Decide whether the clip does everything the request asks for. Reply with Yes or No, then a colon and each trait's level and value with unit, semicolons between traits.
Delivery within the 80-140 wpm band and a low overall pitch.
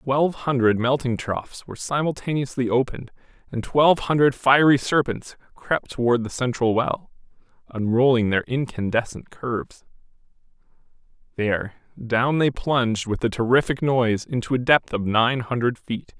Yes: slow, 135 wpm; low, 125 Hz